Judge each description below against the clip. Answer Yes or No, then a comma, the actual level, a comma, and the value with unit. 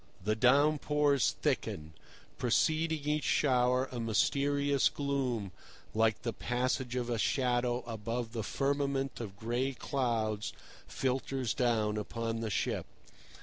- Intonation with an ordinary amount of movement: Yes, average, 3.5 semitones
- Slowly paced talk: Yes, slow, 120 wpm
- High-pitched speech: No, low, 125 Hz